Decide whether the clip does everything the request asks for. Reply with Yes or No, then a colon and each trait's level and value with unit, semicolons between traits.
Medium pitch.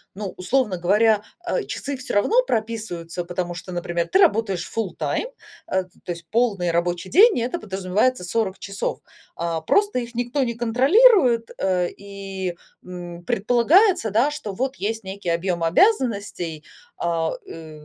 No: high, 200 Hz